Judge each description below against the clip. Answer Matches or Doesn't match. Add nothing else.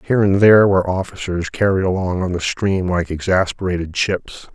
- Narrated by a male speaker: Matches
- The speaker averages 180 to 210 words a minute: Doesn't match